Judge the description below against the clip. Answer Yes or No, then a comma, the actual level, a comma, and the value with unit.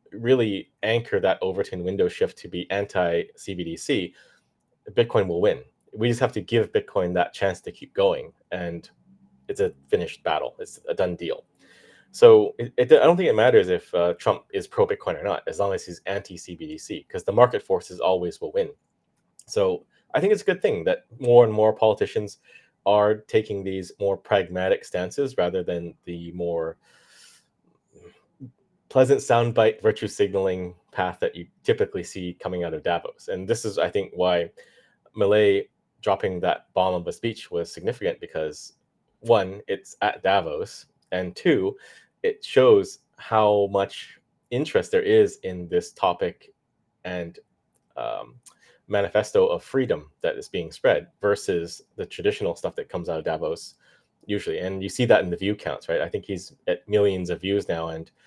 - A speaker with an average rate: Yes, average, 170 wpm